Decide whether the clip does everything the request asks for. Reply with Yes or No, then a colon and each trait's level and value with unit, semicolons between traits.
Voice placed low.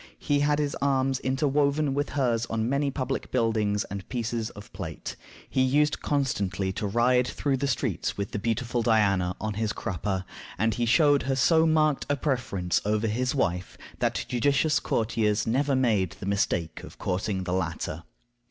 Yes: low, 120 Hz